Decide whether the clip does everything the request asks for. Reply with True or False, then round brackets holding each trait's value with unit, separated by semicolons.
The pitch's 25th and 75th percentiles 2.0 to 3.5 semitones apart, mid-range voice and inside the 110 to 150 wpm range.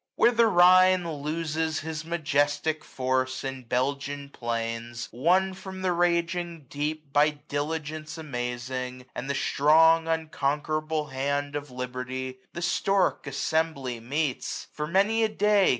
False (4.0 semitones; 150 Hz; 135 wpm)